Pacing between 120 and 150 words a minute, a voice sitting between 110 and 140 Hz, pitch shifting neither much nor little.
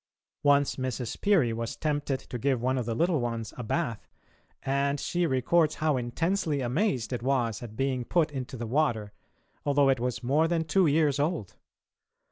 No: average, 175 wpm; low, 135 Hz; average, 4.2 semitones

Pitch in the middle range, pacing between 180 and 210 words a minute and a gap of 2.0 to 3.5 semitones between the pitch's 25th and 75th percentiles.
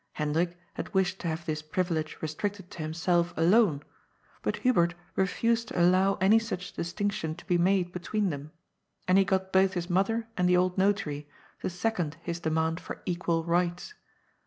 No: medium, 180 Hz; average, 170 wpm; average, 2.7 semitones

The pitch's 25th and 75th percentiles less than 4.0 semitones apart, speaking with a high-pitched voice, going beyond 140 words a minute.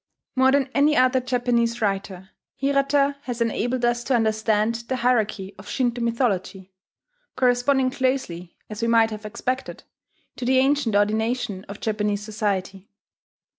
No: average, 3.6 semitones; high, 235 Hz; slow, 135 wpm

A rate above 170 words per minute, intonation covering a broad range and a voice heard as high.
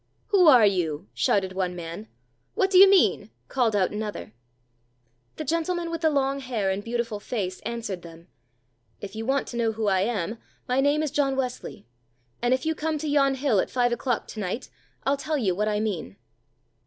Yes: average, 195 wpm; wide, 5.7 semitones; high, 235 Hz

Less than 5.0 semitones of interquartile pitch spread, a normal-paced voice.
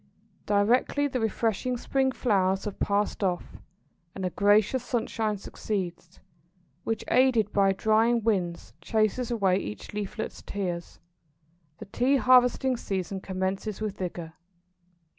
No: average, 3.8 semitones; slow, 120 wpm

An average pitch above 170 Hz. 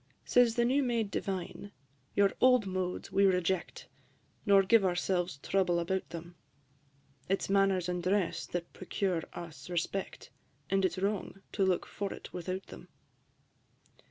Yes: high, 190 Hz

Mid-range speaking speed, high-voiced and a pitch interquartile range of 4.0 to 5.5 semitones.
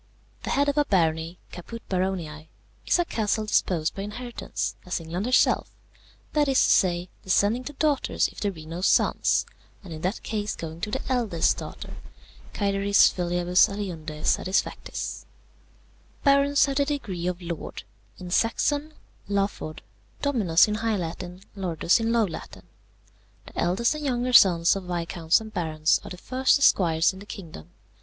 Yes: average, 160 wpm; high, 195 Hz; average, 5.2 semitones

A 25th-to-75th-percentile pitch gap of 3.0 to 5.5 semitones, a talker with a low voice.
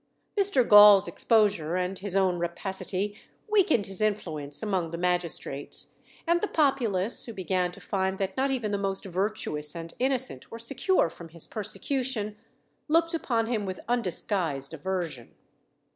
No: average, 4.7 semitones; high, 195 Hz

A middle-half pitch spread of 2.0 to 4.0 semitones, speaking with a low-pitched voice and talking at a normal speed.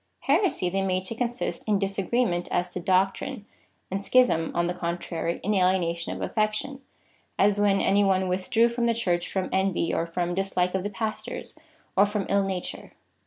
No: average, 2.9 semitones; high, 195 Hz; average, 180 wpm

